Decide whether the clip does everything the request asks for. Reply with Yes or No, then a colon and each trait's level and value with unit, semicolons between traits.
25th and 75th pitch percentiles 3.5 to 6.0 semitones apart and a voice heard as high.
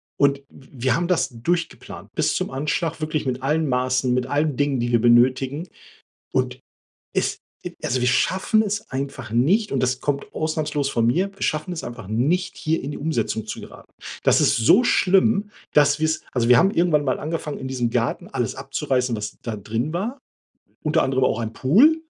No: average, 4.5 semitones; medium, 140 Hz